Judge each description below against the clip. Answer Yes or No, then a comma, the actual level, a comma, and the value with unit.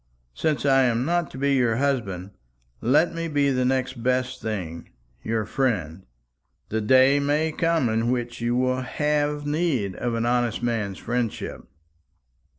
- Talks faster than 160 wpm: No, average, 155 wpm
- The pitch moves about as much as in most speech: Yes, average, 3.7 semitones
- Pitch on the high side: No, low, 125 Hz